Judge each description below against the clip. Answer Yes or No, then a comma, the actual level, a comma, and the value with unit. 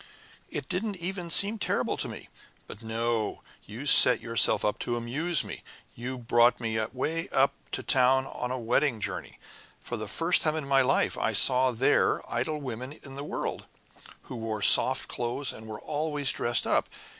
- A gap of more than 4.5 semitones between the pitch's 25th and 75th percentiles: No, average, 4.0 semitones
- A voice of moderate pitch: No, low, 130 Hz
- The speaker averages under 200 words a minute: Yes, average, 175 wpm